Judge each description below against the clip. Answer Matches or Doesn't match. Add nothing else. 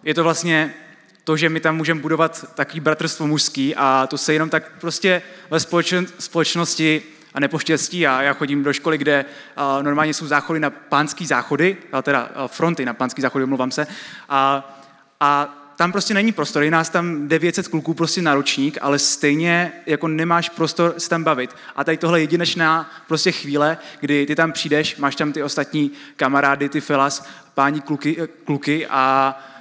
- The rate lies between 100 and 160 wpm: Doesn't match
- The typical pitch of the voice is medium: Matches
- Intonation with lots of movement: Doesn't match